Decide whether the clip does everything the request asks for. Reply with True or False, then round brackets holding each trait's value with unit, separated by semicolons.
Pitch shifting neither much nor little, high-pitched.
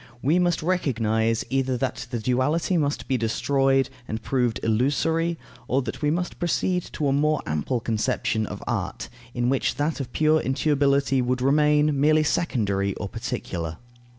False (4.3 semitones; 135 Hz)